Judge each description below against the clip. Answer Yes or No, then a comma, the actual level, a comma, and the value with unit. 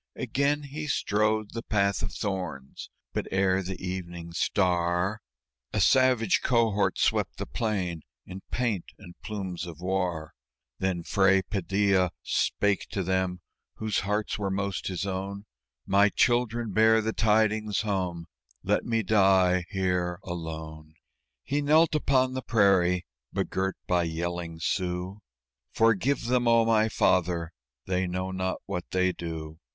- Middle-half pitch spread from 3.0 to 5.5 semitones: Yes, average, 3.4 semitones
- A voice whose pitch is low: Yes, very low, 95 Hz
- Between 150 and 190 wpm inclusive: No, slow, 135 wpm